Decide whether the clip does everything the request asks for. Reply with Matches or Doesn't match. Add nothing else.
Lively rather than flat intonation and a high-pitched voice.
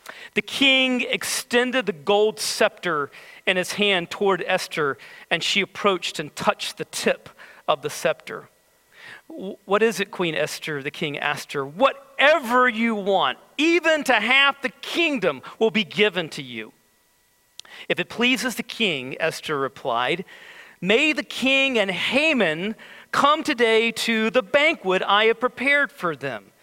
Matches